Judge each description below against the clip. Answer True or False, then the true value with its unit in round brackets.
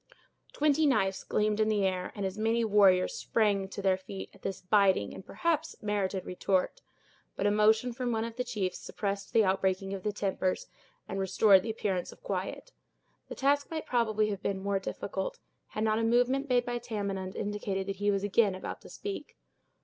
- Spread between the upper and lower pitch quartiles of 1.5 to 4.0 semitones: True (3.2 semitones)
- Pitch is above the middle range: True (205 Hz)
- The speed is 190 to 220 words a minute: True (195 wpm)